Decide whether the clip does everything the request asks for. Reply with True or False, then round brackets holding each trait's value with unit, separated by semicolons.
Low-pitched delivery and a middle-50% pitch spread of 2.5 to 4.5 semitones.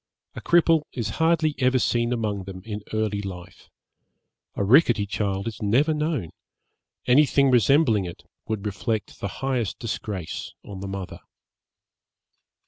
False (110 Hz; 5.2 semitones)